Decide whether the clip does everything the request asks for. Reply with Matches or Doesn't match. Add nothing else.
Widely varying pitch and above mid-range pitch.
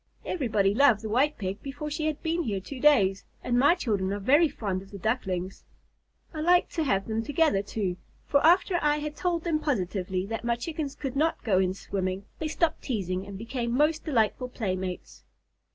Matches